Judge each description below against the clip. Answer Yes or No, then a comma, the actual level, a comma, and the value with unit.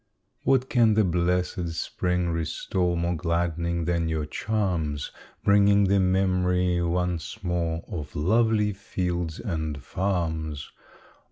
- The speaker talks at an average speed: No, slow, 110 wpm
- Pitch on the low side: Yes, very low, 90 Hz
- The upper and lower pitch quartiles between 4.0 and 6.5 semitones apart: No, narrow, 2.5 semitones